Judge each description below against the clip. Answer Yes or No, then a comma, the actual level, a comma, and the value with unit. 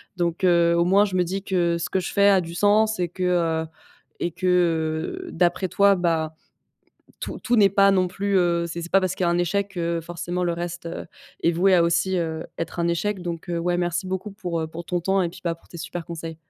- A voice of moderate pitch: Yes, medium, 175 Hz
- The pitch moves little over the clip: Yes, narrow, 2.1 semitones